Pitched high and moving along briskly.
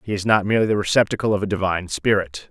No: low, 100 Hz; fast, 240 wpm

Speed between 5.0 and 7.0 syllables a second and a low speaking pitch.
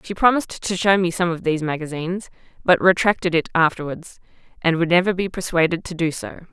No: 6.1 syllables/s; medium, 175 Hz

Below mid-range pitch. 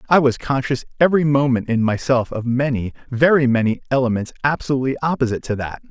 Yes: low, 130 Hz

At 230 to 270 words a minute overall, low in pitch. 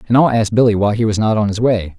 No: fast, 335 wpm; low, 110 Hz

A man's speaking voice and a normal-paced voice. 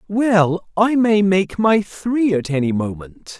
Yes: male; average, 160 wpm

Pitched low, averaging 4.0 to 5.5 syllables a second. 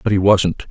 Yes: low, 100 Hz; 4.6 syllables/s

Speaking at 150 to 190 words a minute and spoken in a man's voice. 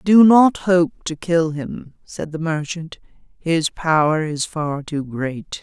No: average, 160 wpm; female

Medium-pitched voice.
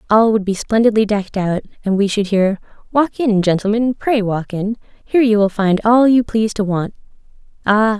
No: high, 210 Hz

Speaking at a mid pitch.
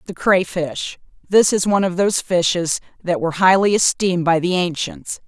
Yes: medium, 180 Hz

